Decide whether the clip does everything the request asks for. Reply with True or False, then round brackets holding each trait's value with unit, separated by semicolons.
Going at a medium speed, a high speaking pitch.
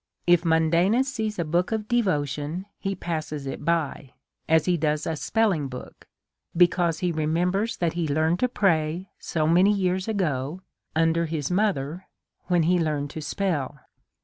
False (155 wpm; 170 Hz)